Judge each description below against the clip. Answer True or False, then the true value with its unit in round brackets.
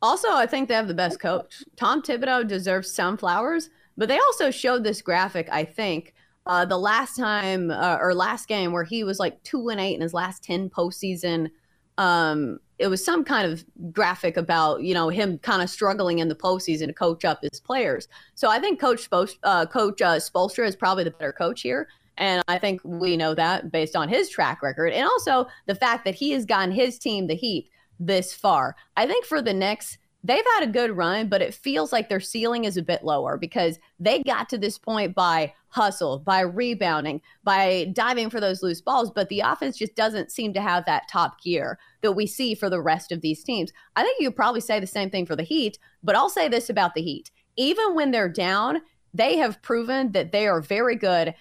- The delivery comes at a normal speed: False (220 wpm)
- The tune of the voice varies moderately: True (5.0 semitones)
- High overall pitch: True (195 Hz)